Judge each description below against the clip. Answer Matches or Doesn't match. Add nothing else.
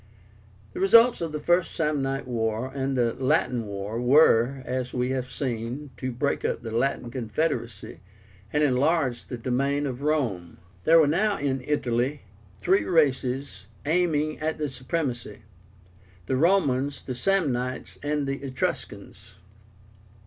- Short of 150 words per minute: Matches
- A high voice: Doesn't match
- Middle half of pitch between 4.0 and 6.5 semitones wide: Doesn't match